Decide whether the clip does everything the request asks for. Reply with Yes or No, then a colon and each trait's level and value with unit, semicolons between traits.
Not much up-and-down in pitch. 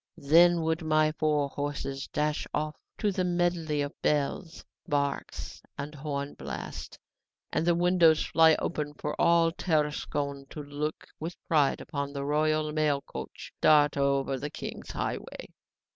Yes: narrow, 2.2 semitones